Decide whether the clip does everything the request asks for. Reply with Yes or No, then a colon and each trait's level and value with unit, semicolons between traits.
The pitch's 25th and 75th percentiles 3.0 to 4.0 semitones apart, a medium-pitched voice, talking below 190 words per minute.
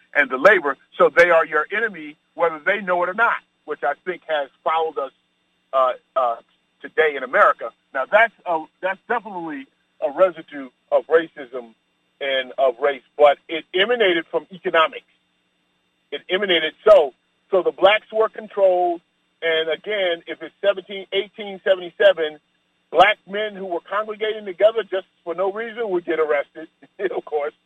No: average, 4.6 semitones; medium, 170 Hz; average, 155 wpm